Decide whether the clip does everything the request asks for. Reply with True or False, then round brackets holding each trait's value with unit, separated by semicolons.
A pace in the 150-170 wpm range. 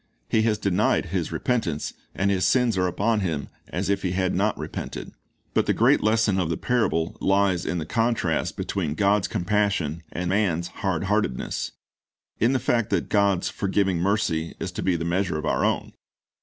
False (185 wpm)